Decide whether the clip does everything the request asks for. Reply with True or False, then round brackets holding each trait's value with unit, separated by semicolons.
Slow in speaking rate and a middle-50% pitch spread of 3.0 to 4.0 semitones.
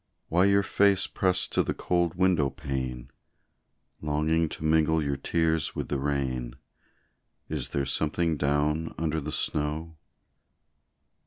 False (130 wpm; 2.6 semitones)